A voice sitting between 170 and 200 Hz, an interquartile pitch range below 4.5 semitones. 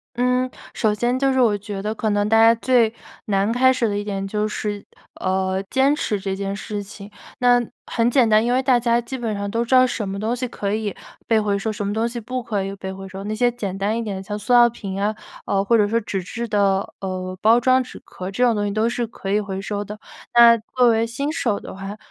No: high, 215 Hz; average, 3.1 semitones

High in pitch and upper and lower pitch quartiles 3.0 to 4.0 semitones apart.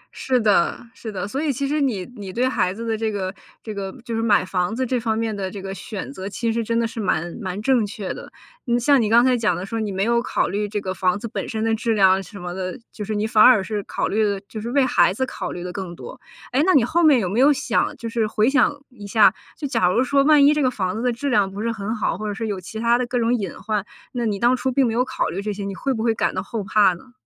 Yes: high, 220 Hz; average, 3.7 semitones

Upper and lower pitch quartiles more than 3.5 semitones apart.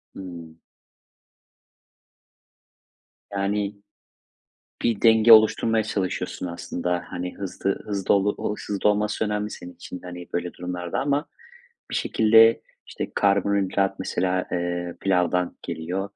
No: average, 2.9 semitones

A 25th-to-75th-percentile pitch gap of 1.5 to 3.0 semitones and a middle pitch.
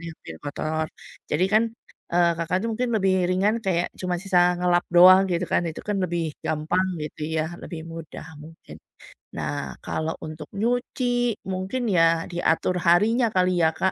Yes: average, 2.7 semitones; medium, 175 Hz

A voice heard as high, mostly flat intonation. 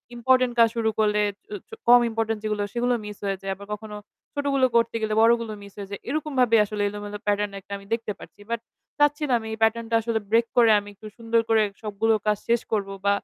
Yes: high, 225 Hz; narrow, 2.0 semitones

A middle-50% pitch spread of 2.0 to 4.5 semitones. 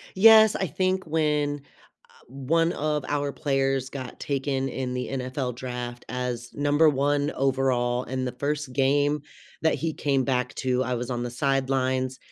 Yes: narrow, 2.4 semitones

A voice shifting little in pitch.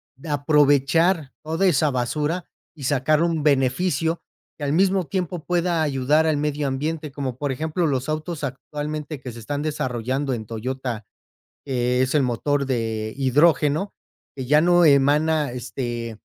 No: average, 3.3 semitones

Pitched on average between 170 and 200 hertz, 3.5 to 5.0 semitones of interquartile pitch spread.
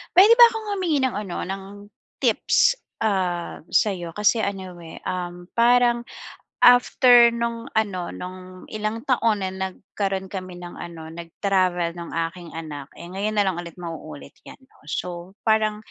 Yes: high, 190 Hz; average, 4.5 semitones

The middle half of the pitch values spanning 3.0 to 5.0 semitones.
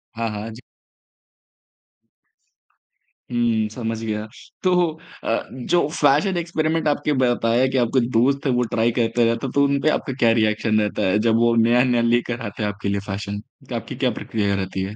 Yes: average, 3.3 semitones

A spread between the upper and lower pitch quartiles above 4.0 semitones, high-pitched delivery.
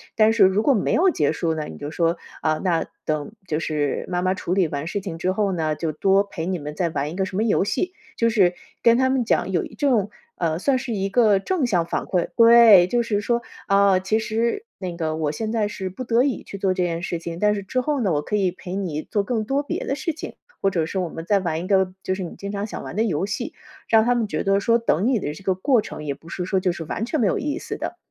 Yes: average, 4.9 semitones; high, 195 Hz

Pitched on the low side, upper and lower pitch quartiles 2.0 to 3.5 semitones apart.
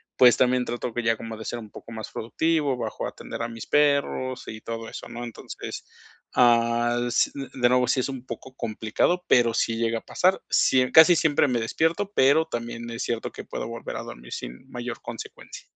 Yes: low, 120 Hz; narrow, 2.5 semitones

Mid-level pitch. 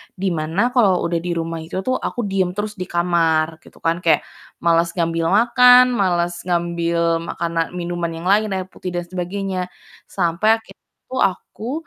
Yes: medium, 175 Hz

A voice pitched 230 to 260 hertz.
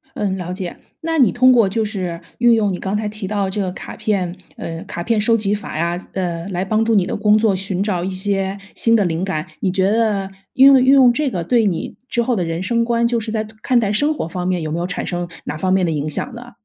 No: high, 200 Hz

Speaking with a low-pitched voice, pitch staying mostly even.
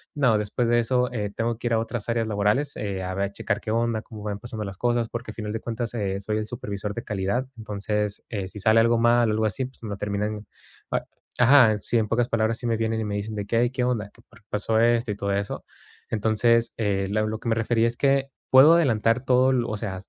Yes: low, 110 Hz; narrow, 2.2 semitones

